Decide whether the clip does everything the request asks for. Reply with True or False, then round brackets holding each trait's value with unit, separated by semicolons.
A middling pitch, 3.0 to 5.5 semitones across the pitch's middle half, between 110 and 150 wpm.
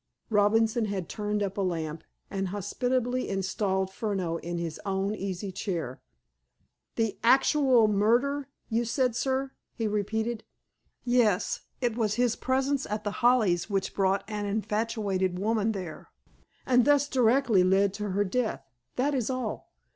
False (210 Hz; 4.0 semitones; 140 wpm)